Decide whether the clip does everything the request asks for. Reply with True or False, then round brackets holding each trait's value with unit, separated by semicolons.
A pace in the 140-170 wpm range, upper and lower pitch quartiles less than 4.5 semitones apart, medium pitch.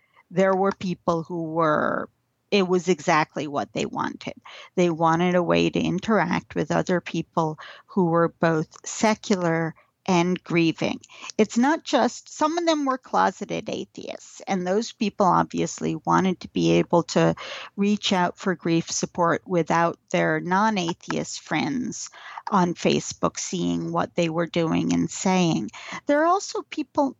True (150 wpm; 4.0 semitones; 175 Hz)